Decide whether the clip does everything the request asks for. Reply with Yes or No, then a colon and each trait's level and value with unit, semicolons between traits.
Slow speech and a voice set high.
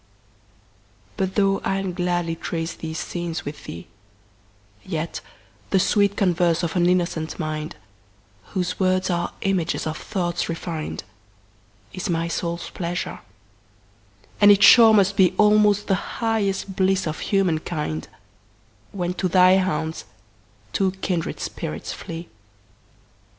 No: slow, 110 wpm; medium, 170 Hz